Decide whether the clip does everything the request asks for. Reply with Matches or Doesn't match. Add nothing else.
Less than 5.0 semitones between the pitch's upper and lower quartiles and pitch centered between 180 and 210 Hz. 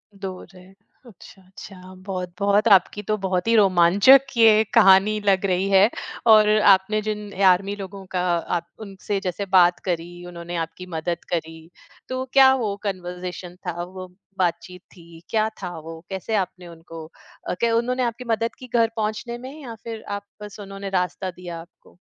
Matches